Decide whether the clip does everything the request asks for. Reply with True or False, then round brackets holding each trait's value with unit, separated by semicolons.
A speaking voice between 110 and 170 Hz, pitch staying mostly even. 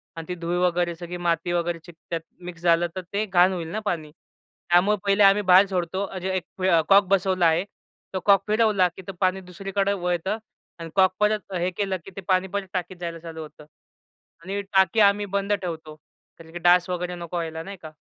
False (180 Hz; 2.3 semitones)